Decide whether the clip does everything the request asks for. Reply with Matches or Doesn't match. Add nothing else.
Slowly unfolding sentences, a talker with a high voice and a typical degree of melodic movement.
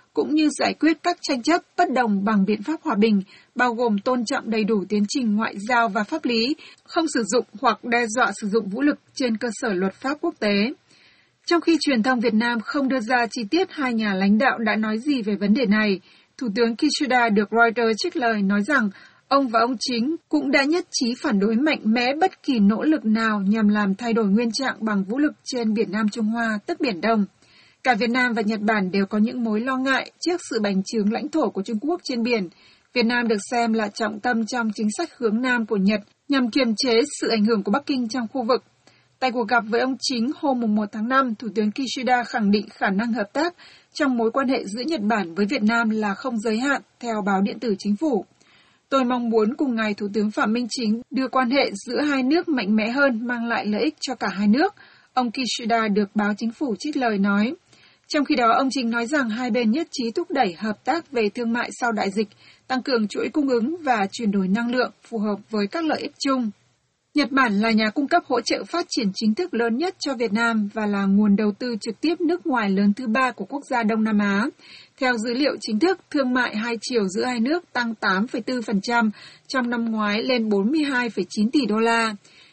Doesn't match